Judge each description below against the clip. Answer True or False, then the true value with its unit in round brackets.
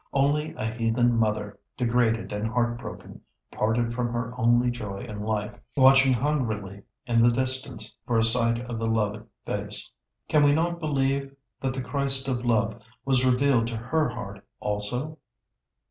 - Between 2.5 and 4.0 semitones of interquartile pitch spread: True (3.0 semitones)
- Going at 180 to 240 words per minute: False (160 wpm)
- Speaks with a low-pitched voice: True (120 Hz)